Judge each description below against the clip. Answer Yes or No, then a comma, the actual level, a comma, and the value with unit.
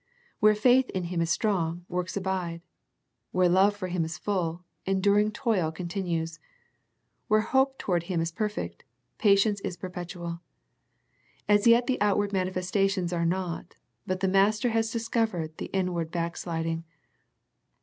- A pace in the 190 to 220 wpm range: No, average, 145 wpm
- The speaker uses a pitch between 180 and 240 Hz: Yes, medium, 185 Hz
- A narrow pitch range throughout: No, average, 3.3 semitones